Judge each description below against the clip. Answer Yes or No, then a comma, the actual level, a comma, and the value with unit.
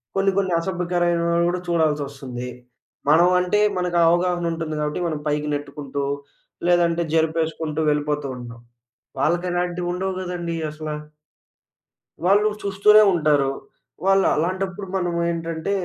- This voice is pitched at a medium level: Yes, medium, 170 Hz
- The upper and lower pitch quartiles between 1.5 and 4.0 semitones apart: Yes, average, 2.8 semitones